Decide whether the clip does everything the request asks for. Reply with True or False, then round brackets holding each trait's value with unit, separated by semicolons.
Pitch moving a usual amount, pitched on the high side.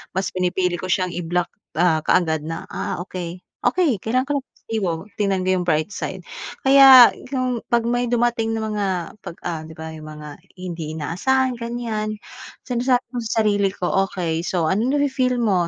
False (5.7 semitones; 195 Hz)